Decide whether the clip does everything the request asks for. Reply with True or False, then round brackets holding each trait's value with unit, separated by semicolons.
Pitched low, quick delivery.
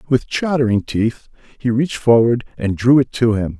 False (120 Hz; 185 wpm)